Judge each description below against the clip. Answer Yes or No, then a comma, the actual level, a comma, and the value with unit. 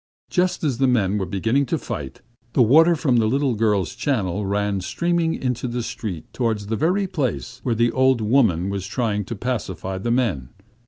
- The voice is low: Yes, low, 115 Hz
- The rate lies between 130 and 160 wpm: No, average, 190 wpm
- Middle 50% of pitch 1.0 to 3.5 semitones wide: No, average, 4.8 semitones